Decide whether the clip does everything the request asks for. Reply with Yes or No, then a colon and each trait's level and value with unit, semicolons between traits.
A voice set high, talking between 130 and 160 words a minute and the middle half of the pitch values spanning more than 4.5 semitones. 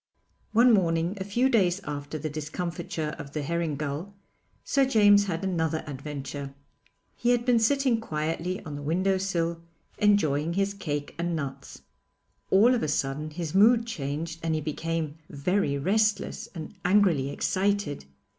No: medium, 170 Hz; average, 150 wpm; average, 5.0 semitones